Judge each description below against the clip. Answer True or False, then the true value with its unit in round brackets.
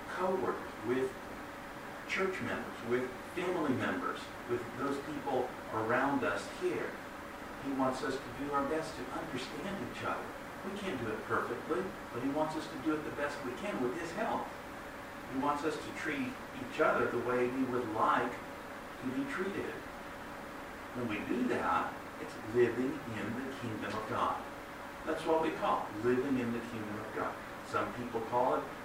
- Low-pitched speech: True (130 Hz)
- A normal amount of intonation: True (3.1 semitones)